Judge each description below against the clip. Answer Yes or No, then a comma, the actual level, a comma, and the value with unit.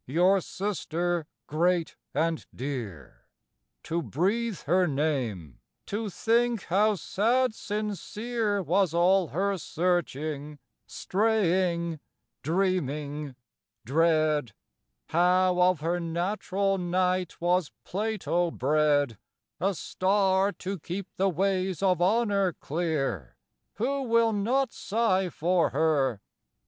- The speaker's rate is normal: No, slow, 100 wpm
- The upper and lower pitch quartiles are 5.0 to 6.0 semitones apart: No, average, 4.2 semitones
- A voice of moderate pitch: Yes, medium, 180 Hz